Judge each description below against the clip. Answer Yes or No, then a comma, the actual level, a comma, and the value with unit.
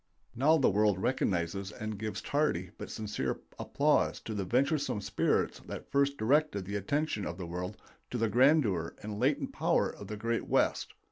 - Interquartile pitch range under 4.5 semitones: No, wide, 5.6 semitones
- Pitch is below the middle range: Yes, low, 105 Hz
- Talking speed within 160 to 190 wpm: Yes, average, 175 wpm